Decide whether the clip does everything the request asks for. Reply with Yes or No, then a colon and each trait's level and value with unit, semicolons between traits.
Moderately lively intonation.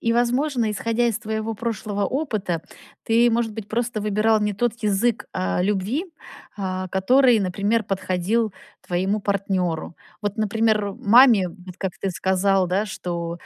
Yes: average, 3.3 semitones